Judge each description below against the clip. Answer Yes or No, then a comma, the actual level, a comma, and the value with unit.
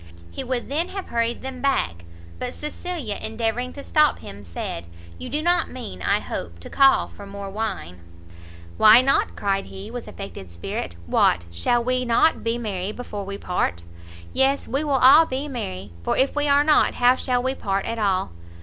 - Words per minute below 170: No, average, 185 wpm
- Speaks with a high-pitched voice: Yes, high, 235 Hz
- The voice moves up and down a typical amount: No, wide, 5.7 semitones